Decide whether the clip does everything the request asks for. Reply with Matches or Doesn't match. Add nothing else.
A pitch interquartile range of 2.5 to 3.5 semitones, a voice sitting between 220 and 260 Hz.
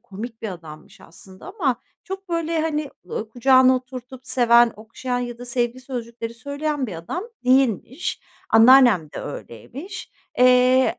Matches